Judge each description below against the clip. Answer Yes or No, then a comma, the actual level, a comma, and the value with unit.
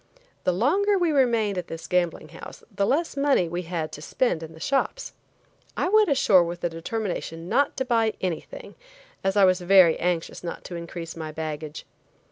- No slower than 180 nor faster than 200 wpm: Yes, average, 185 wpm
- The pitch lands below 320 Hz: Yes, medium, 185 Hz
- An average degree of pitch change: No, wide, 7.9 semitones